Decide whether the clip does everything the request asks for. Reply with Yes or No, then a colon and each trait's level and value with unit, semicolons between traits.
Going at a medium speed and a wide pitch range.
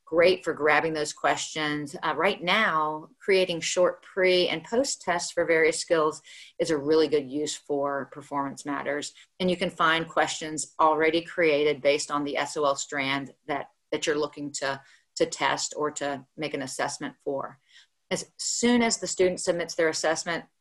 No: average, 170 wpm; average, 2.9 semitones